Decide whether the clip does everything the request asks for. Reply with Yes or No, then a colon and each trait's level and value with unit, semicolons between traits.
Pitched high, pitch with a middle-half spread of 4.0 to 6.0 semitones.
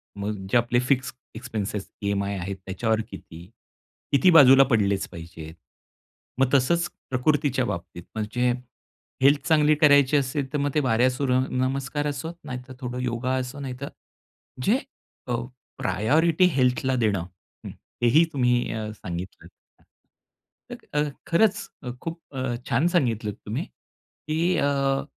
No: low, 125 Hz; average, 4.5 semitones